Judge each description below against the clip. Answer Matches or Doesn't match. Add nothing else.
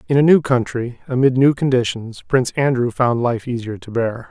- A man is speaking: Matches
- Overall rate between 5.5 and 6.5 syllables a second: Doesn't match